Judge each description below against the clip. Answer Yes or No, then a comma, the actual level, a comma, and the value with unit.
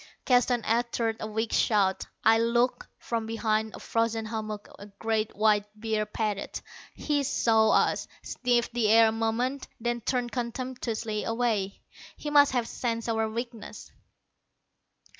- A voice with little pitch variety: Yes, narrow, 1.7 semitones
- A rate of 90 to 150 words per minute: Yes, average, 140 wpm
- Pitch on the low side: No, high, 225 Hz